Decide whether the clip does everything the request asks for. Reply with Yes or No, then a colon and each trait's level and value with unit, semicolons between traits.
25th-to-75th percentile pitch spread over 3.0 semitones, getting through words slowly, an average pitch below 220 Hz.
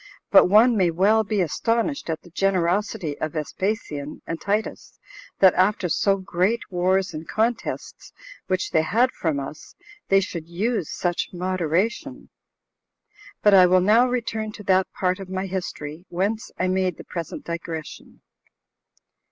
No: average, 3.7 semitones; average, 145 wpm; medium, 185 Hz